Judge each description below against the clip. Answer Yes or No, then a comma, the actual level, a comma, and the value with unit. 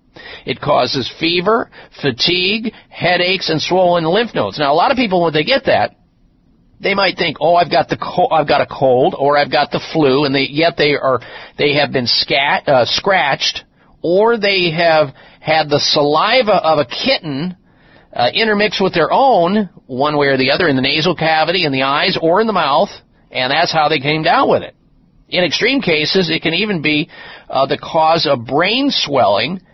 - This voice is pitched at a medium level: Yes, medium, 165 Hz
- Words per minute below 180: No, average, 195 wpm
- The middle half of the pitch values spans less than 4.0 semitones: No, average, 4.3 semitones